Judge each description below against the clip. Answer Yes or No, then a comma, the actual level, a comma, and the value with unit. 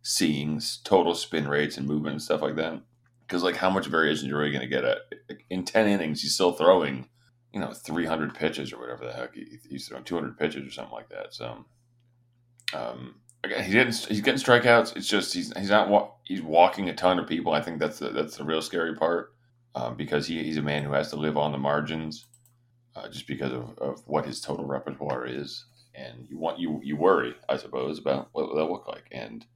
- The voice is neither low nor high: No, very low, 80 Hz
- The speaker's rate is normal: No, fast, 230 wpm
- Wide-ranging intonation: Yes, wide, 8.5 semitones